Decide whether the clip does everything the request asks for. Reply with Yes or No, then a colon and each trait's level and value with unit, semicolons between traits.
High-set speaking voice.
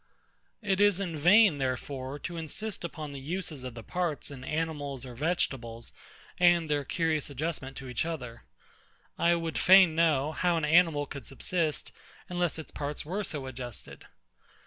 No: medium, 155 Hz